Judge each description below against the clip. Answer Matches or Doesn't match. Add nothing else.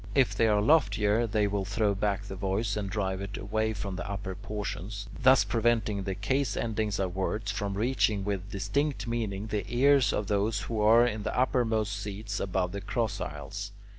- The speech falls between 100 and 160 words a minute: Doesn't match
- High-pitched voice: Doesn't match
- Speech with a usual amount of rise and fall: Doesn't match